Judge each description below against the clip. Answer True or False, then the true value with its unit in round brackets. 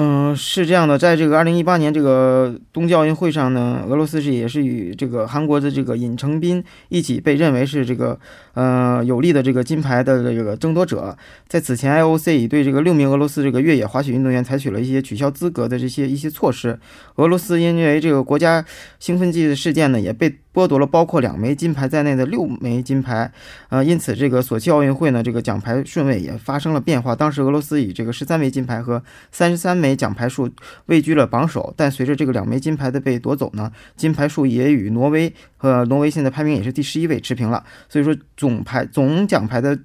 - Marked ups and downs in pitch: False (3.6 semitones)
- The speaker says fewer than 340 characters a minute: False (345 characters per minute)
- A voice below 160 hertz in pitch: True (140 Hz)